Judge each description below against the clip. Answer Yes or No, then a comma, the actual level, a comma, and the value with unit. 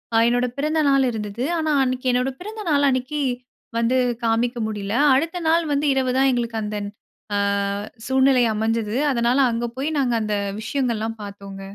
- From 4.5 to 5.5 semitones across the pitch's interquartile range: No, average, 3.3 semitones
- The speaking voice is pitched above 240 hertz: Yes, very high, 250 Hz